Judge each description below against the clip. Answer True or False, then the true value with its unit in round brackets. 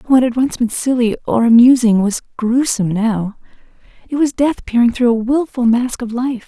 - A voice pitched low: False (240 Hz)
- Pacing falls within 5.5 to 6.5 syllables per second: False (5.0 syllables/s)